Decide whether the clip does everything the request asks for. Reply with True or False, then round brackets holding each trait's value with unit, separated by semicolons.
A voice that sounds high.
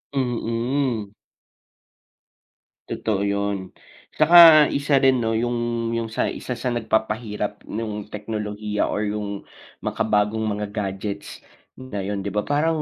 False (110 Hz)